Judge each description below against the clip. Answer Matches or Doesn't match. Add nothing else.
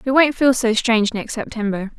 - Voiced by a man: Doesn't match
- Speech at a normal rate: Doesn't match